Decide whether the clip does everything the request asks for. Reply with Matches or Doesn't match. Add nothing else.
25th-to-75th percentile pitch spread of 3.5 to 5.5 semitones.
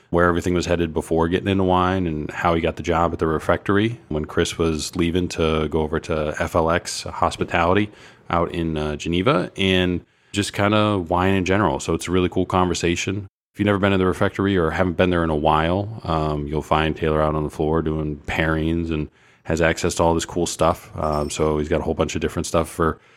Doesn't match